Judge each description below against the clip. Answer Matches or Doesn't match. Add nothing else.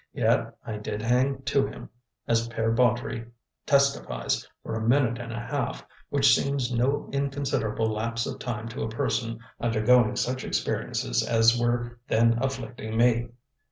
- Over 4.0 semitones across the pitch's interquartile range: Doesn't match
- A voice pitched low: Matches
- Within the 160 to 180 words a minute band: Doesn't match